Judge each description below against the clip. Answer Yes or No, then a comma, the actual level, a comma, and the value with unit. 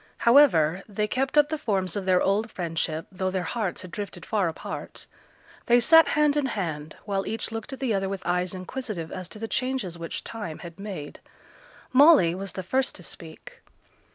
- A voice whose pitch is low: No, high, 195 Hz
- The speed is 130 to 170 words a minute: No, average, 190 wpm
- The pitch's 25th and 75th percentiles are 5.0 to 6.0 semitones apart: Yes, average, 5.3 semitones